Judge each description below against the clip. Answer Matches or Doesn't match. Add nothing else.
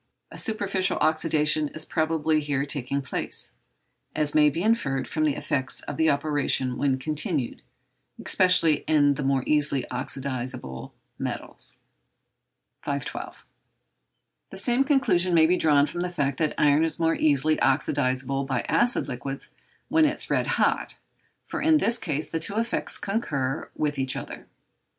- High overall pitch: Doesn't match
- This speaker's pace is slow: Doesn't match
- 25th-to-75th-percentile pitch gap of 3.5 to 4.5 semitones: Matches